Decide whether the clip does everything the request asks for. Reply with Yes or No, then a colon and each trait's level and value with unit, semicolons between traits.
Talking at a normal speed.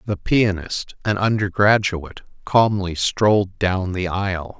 No: slow, 115 wpm